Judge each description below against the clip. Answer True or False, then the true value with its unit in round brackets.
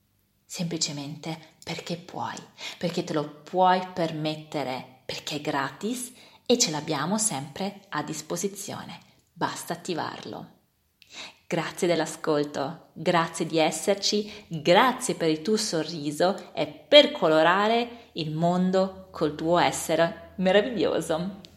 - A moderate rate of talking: False (105 wpm)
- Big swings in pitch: False (3.9 semitones)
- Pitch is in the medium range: True (165 Hz)